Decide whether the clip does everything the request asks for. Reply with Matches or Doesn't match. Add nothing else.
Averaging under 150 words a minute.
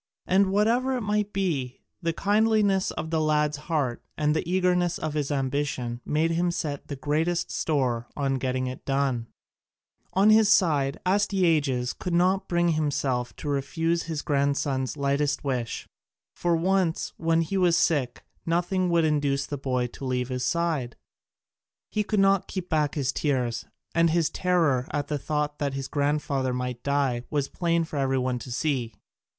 Doesn't match